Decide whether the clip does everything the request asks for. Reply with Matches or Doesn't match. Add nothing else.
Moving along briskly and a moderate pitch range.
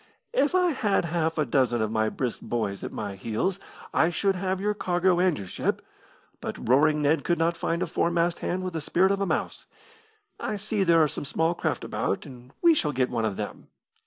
Doesn't match